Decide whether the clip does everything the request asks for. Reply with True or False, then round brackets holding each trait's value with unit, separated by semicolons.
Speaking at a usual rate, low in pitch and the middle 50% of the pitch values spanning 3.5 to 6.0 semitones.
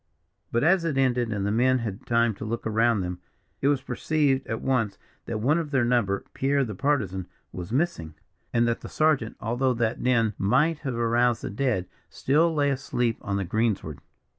True (190 wpm; 120 Hz; 3.9 semitones)